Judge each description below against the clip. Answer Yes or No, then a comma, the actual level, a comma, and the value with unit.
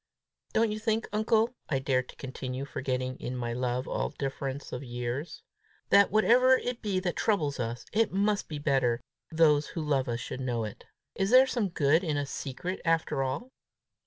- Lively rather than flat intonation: Yes, wide, 7.9 semitones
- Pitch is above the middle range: No, medium, 145 Hz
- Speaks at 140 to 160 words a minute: No, average, 185 wpm